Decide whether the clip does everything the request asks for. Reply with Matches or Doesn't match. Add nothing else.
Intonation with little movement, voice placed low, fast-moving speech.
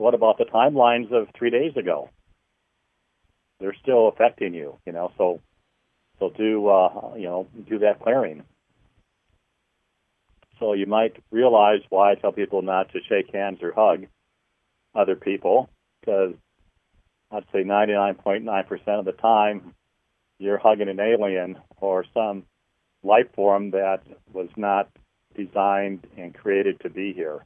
Doesn't match